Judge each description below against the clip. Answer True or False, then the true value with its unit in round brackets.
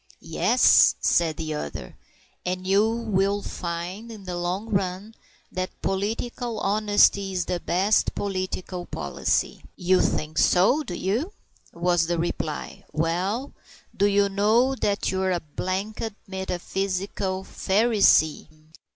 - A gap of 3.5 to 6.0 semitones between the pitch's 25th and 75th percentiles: False (2.7 semitones)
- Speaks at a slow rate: True (120 wpm)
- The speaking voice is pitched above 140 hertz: True (190 Hz)